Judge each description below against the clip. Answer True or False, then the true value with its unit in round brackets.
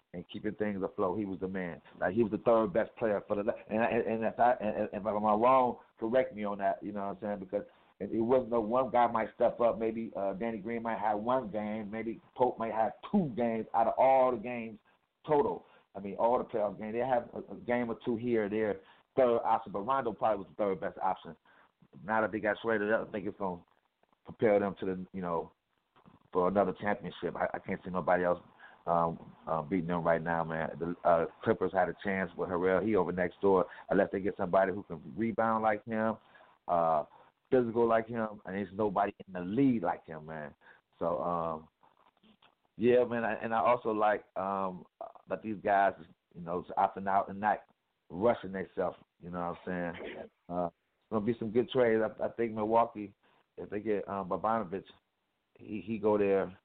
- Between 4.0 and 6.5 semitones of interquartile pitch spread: False (3.2 semitones)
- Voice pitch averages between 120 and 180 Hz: False (105 Hz)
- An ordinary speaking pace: False (215 wpm)